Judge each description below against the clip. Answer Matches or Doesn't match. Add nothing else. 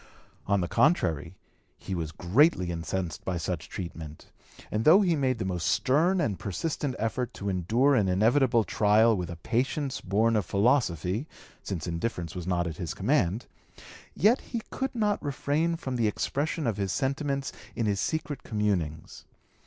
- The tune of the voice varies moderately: Doesn't match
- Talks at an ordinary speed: Matches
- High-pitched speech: Doesn't match